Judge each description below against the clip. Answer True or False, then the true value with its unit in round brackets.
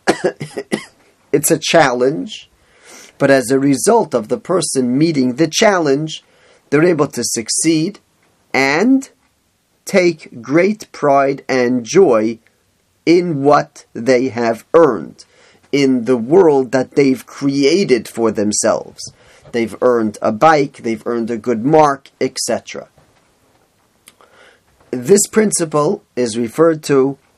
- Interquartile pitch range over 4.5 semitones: True (5.2 semitones)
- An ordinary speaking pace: False (110 wpm)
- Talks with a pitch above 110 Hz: True (135 Hz)